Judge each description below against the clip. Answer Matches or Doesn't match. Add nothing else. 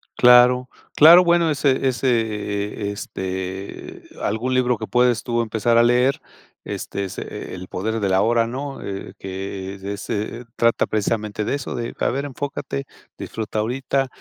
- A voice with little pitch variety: Doesn't match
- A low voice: Matches